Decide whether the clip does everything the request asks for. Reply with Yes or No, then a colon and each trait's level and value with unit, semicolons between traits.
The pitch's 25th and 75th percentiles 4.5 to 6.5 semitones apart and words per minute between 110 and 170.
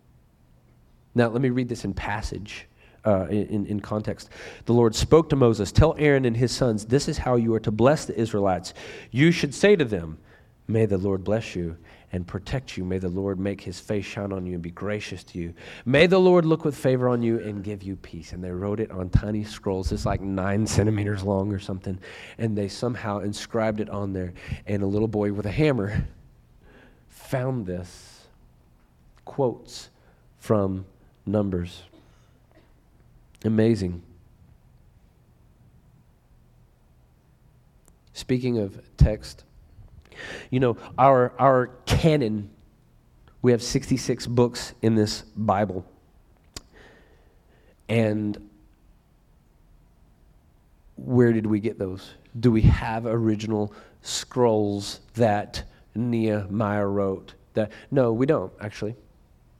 No: average, 3.8 semitones; average, 140 wpm